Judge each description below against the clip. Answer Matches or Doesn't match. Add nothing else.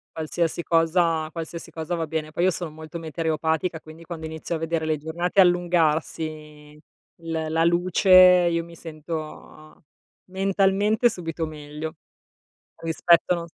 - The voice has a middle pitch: Matches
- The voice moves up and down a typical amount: Doesn't match